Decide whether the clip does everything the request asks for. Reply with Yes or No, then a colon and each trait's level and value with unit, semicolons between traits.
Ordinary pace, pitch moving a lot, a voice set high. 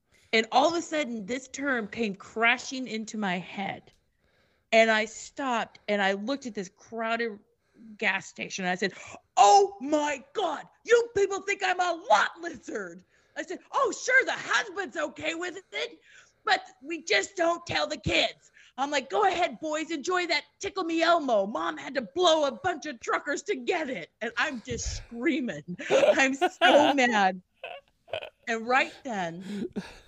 Yes: average, 165 wpm; wide, 7.3 semitones; very high, 275 Hz